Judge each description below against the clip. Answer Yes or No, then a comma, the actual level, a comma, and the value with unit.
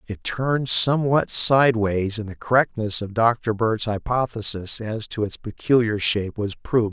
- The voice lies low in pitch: Yes, low, 110 Hz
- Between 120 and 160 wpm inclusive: Yes, average, 155 wpm